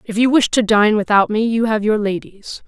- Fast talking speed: Yes, fast, 245 wpm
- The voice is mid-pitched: No, high, 215 Hz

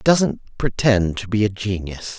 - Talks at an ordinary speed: Yes, average, 190 wpm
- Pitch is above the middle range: No, low, 105 Hz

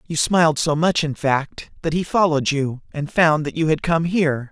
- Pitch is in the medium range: Yes, medium, 155 Hz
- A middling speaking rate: No, fast, 225 wpm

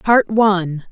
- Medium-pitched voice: No, high, 195 Hz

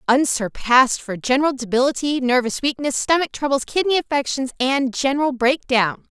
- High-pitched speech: Yes, very high, 265 Hz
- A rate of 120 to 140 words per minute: Yes, slow, 135 wpm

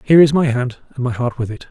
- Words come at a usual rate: No, fast, 315 wpm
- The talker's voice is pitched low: Yes, low, 130 Hz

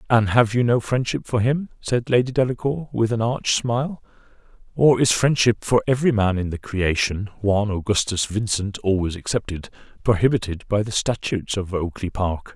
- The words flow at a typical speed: Yes, average, 165 wpm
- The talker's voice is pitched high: No, low, 110 Hz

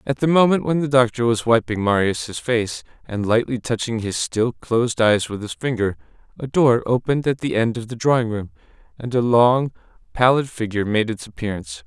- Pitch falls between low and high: No, low, 120 Hz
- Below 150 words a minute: No, average, 190 wpm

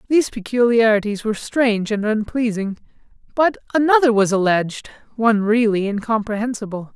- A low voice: No, high, 225 Hz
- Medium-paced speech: No, slow, 110 wpm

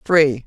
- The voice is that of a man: No, female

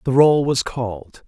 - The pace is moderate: Yes, average, 190 wpm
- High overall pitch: No, low, 125 Hz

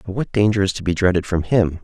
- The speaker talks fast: Yes, fast, 295 wpm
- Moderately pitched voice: No, very low, 95 Hz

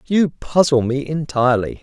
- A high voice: No, medium, 145 Hz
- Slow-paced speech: Yes, slow, 130 wpm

